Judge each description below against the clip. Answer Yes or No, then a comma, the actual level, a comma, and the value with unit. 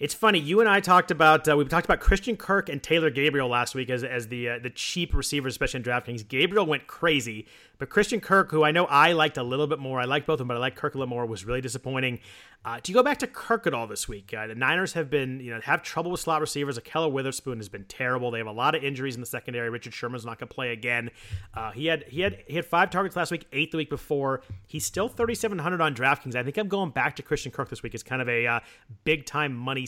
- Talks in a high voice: No, medium, 140 Hz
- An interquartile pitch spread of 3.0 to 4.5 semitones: No, average, 5.0 semitones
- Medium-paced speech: No, fast, 280 wpm